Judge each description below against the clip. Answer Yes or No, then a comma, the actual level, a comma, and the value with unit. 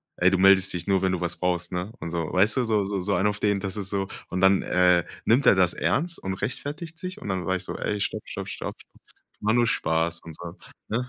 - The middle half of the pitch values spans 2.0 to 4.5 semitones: Yes, average, 2.7 semitones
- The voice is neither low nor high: No, very low, 95 Hz